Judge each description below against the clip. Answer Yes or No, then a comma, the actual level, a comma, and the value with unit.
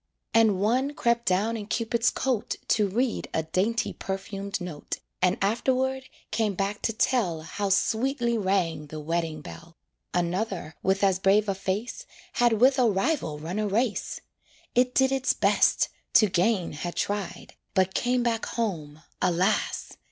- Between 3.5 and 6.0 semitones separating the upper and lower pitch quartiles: Yes, average, 4.5 semitones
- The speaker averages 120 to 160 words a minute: Yes, average, 150 wpm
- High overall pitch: Yes, high, 205 Hz